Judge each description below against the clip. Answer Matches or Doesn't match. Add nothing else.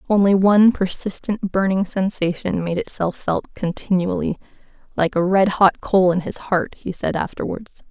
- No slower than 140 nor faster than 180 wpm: Matches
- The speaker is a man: Doesn't match